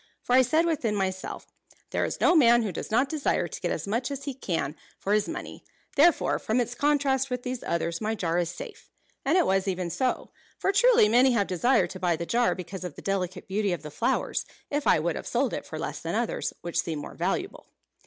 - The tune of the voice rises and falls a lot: Yes, wide, 6.7 semitones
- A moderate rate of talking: No, fast, 230 wpm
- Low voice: No, high, 220 Hz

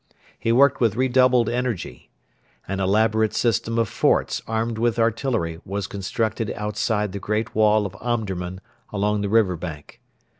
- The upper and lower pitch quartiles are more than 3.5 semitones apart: No, average, 2.7 semitones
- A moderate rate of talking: Yes, average, 145 wpm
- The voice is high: No, low, 110 Hz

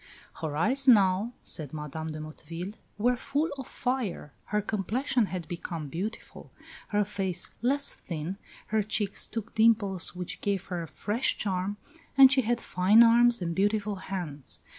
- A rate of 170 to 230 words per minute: No, average, 155 wpm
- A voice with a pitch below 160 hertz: No, high, 200 Hz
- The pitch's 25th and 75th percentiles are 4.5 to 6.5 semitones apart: Yes, average, 4.9 semitones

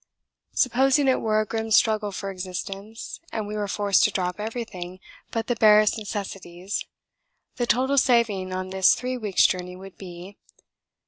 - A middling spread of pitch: Yes, average, 3.2 semitones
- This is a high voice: Yes, high, 210 Hz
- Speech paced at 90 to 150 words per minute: No, average, 165 wpm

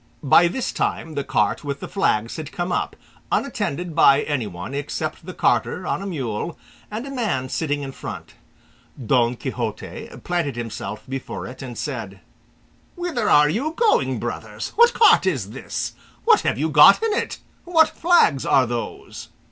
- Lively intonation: Yes, wide, 7.8 semitones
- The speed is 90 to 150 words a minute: No, average, 165 wpm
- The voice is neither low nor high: Yes, medium, 150 Hz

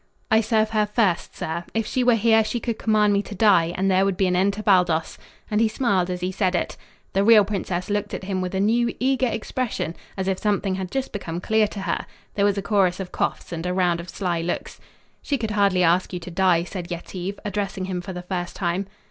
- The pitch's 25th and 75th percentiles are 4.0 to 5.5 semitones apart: No, average, 2.9 semitones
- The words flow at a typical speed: No, fast, 240 wpm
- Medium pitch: No, high, 195 Hz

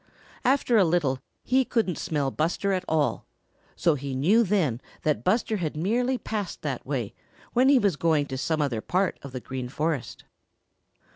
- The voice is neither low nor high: Yes, medium, 165 Hz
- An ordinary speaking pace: Yes, average, 170 wpm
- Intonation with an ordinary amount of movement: No, wide, 7.1 semitones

